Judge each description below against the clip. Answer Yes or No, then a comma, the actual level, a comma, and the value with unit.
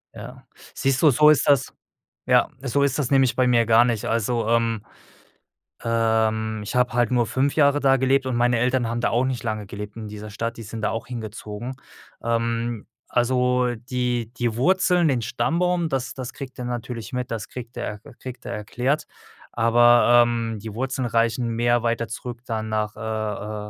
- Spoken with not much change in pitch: Yes, narrow, 2.2 semitones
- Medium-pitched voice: No, low, 120 Hz